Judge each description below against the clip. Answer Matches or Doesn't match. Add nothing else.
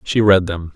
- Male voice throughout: Matches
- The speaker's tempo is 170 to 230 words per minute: Doesn't match